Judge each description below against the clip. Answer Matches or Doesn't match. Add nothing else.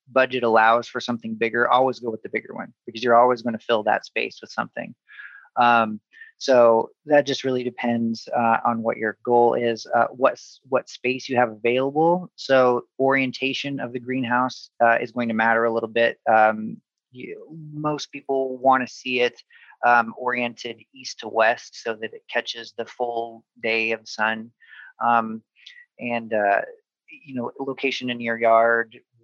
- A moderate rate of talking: Matches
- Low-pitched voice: Matches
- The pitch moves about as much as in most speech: Doesn't match